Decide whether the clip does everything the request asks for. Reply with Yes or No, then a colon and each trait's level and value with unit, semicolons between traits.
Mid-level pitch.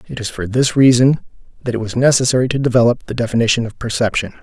No: low, 120 Hz